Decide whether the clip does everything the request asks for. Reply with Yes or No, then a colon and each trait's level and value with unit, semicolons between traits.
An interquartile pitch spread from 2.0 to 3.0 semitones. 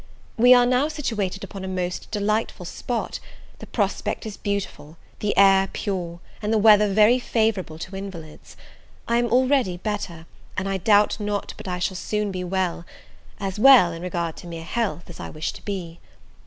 No: average, 3.5 semitones